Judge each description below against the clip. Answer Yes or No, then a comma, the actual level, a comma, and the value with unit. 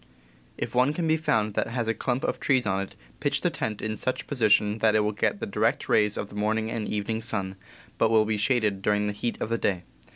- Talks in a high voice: No, low, 110 Hz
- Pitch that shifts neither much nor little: No, narrow, 1.9 semitones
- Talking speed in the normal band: No, fast, 255 wpm